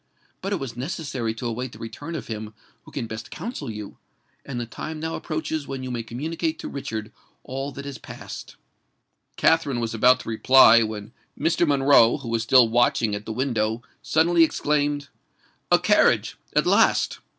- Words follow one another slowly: No, average, 175 wpm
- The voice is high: No, low, 130 Hz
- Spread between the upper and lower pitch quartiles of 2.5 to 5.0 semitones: Yes, average, 4.7 semitones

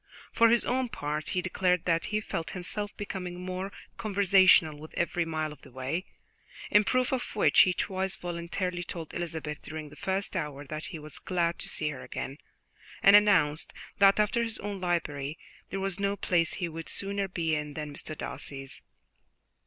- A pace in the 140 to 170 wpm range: No, average, 180 wpm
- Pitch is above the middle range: No, medium, 175 Hz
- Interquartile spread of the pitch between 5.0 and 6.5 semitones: No, average, 4.2 semitones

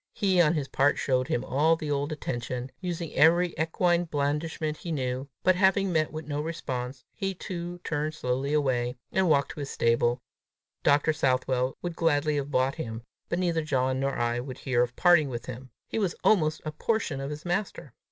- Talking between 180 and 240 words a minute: Yes, average, 190 wpm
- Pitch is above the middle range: No, medium, 150 Hz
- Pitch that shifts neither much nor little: Yes, average, 4.4 semitones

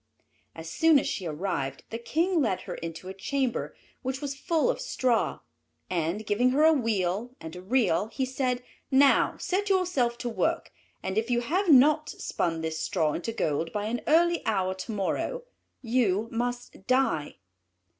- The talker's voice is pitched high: Yes, high, 235 Hz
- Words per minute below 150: No, average, 170 wpm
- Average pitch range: No, wide, 6.7 semitones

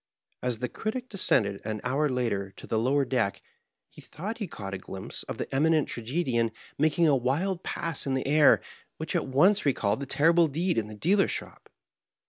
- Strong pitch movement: Yes, wide, 6.2 semitones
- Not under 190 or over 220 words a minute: Yes, average, 195 wpm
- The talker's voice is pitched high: No, low, 135 Hz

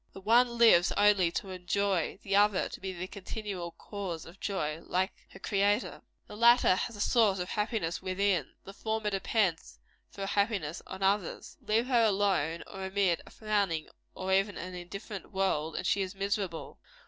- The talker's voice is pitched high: Yes, high, 195 Hz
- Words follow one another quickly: No, average, 175 wpm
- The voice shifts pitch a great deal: No, narrow, 2.4 semitones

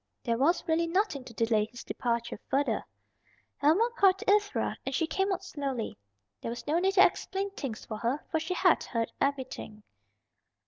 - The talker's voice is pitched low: No, very high, 290 Hz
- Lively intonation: Yes, wide, 7.8 semitones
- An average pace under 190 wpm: Yes, average, 180 wpm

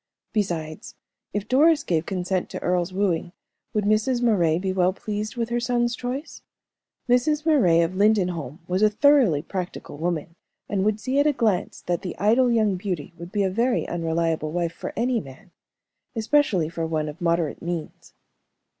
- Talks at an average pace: Yes, average, 170 wpm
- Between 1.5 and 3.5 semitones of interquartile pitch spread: No, wide, 5.5 semitones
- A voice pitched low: No, high, 190 Hz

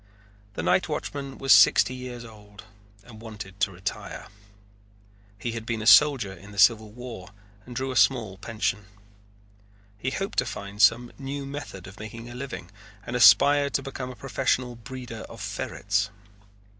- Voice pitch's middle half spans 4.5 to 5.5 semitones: No, average, 3.9 semitones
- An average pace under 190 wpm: Yes, average, 160 wpm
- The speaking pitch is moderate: No, low, 115 Hz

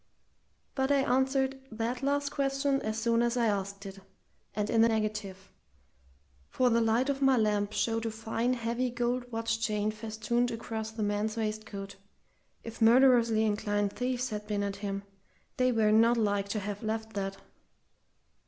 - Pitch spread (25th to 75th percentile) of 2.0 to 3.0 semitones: Yes, narrow, 2.6 semitones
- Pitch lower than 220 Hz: No, high, 225 Hz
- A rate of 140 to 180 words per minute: Yes, average, 160 wpm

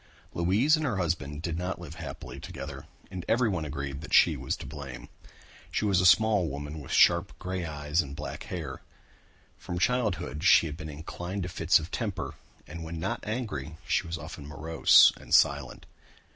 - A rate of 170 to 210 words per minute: Yes, average, 180 wpm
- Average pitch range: Yes, average, 3.9 semitones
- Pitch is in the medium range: No, very low, 85 Hz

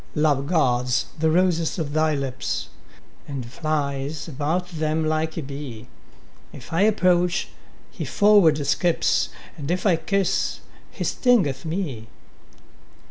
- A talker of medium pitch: Yes, medium, 155 Hz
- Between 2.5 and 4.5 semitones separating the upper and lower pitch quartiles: Yes, average, 4.0 semitones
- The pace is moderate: No, slow, 125 wpm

